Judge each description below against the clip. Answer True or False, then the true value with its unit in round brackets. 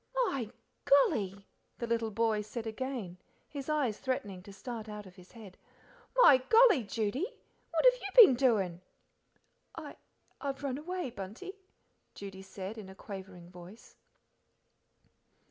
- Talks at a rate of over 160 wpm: False (135 wpm)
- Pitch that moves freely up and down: True (5.8 semitones)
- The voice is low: False (225 Hz)